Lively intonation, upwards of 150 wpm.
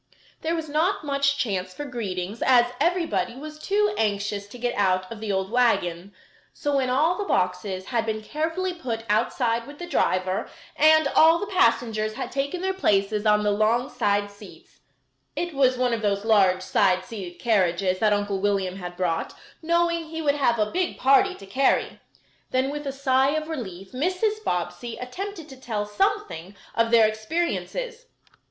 Yes: wide, 7.3 semitones; average, 175 wpm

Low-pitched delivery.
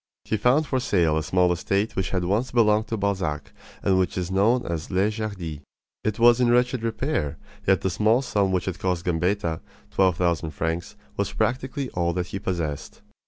Yes: very low, 95 Hz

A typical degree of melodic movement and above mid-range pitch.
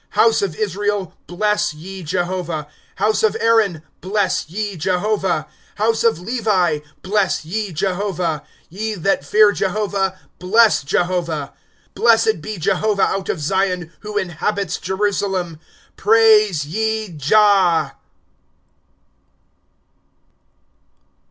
Yes: average, 3.3 semitones; high, 195 Hz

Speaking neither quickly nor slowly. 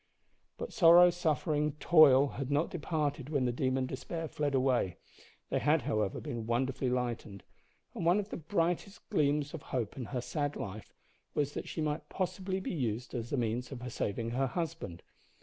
Yes: average, 175 wpm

